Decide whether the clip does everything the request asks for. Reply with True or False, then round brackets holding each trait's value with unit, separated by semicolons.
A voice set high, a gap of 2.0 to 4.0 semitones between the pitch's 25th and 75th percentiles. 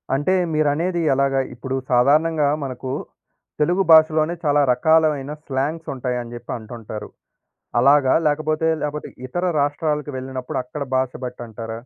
False (140 Hz; 3.5 semitones)